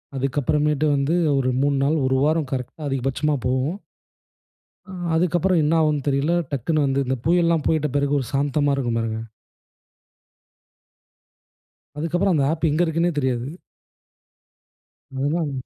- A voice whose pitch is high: No, medium, 145 Hz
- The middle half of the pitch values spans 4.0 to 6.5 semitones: No, average, 3.0 semitones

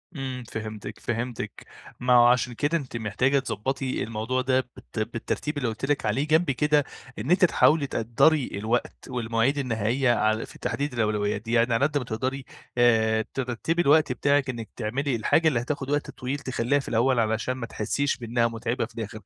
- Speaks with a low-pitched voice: Yes, low, 125 Hz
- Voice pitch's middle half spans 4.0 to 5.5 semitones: No, average, 3.6 semitones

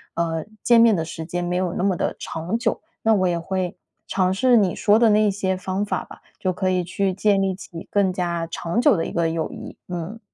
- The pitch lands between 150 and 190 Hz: Yes, medium, 185 Hz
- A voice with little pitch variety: No, average, 3.0 semitones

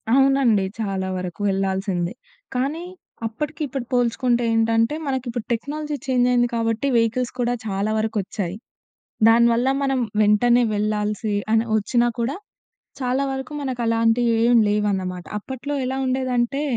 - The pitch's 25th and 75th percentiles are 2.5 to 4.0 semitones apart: Yes, average, 3.4 semitones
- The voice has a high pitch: Yes, high, 235 Hz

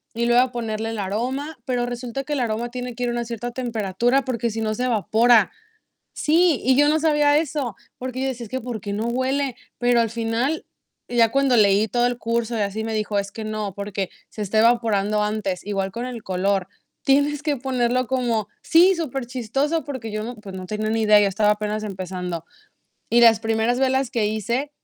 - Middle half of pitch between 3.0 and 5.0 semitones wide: Yes, average, 3.3 semitones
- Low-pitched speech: No, high, 235 Hz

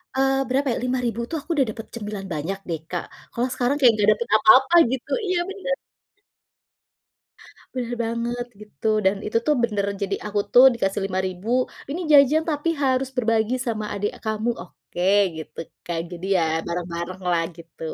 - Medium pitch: No, high, 225 Hz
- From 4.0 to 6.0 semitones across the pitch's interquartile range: Yes, average, 5.1 semitones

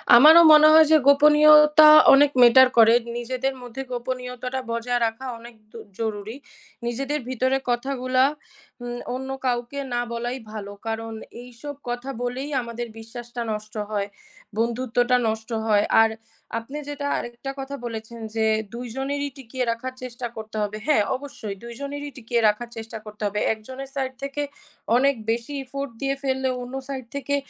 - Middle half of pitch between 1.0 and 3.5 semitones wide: Yes, average, 2.9 semitones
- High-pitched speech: Yes, high, 245 Hz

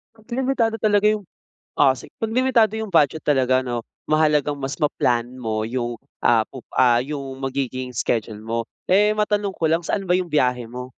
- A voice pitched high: No, medium, 140 Hz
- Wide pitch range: Yes, wide, 8.7 semitones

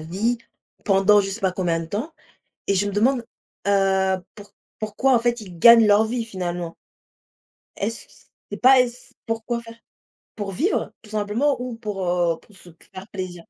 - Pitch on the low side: No, high, 205 Hz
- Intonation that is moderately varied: Yes, average, 3.7 semitones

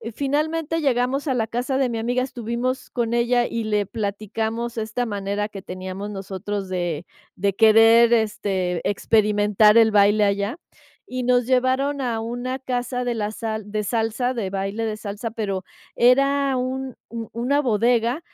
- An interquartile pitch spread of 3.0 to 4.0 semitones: Yes, average, 3.3 semitones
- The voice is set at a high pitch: Yes, high, 225 Hz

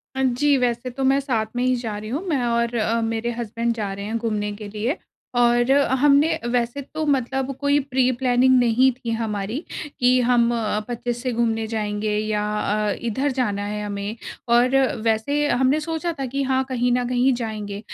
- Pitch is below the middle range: No, high, 240 Hz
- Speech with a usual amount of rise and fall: Yes, average, 3.3 semitones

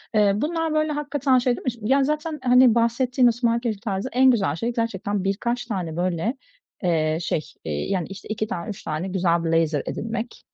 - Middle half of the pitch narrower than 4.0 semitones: No, wide, 5.4 semitones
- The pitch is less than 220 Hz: No, high, 225 Hz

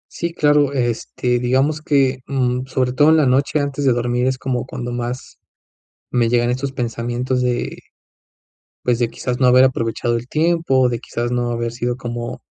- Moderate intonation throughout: No, narrow, 1.9 semitones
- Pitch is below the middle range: Yes, low, 125 Hz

